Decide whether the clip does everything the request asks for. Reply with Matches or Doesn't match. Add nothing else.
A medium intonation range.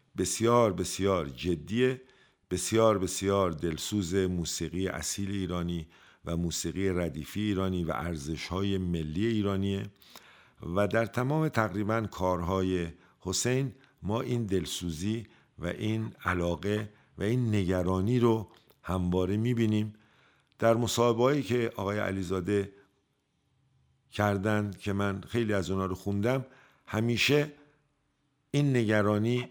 Matches